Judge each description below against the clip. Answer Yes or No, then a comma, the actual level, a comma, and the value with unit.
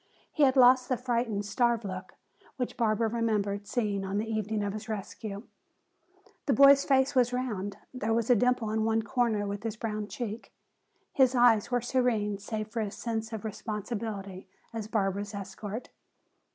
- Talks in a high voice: Yes, high, 220 Hz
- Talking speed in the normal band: Yes, average, 165 wpm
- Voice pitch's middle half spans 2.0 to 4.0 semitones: Yes, average, 2.9 semitones